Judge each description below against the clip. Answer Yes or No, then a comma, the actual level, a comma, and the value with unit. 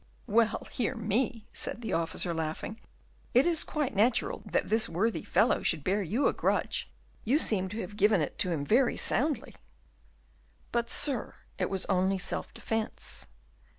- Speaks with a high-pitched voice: Yes, high, 215 Hz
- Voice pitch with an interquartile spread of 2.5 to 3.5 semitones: No, average, 4.4 semitones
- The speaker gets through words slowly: No, average, 160 wpm